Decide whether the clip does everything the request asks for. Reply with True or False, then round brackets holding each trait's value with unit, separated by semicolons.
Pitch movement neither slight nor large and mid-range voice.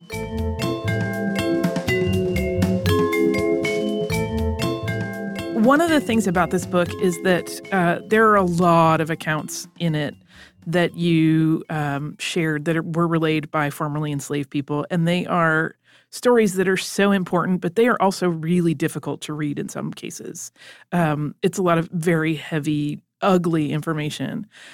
True (4.9 semitones; 160 Hz)